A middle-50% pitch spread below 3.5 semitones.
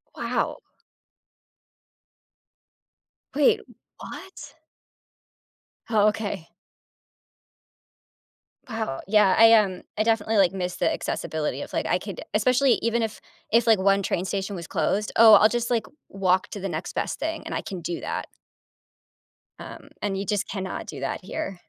Yes: average, 3.0 semitones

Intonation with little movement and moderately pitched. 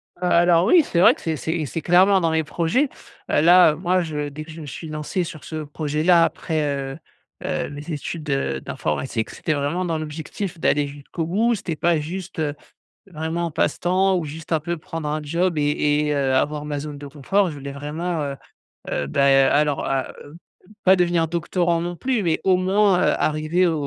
No: average, 3.1 semitones; medium, 160 Hz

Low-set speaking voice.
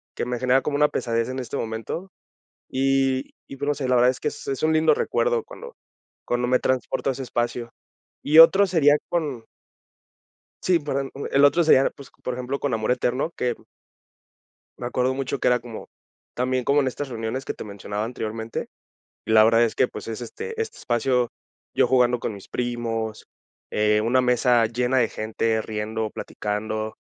Yes: low, 125 Hz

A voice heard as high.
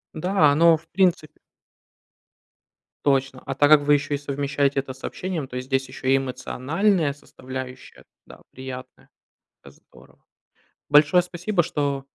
No: medium, 145 Hz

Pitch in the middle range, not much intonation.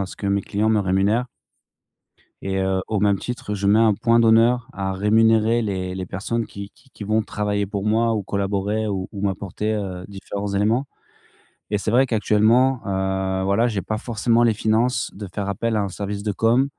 No: low, 105 Hz; narrow, 2.3 semitones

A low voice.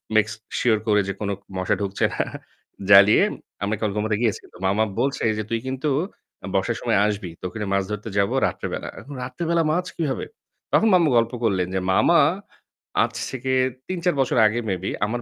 Yes: low, 110 Hz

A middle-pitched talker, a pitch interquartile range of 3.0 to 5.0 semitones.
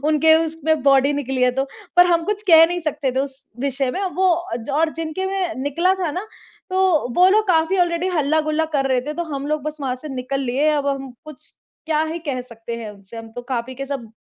No: very high, 300 Hz; average, 3.8 semitones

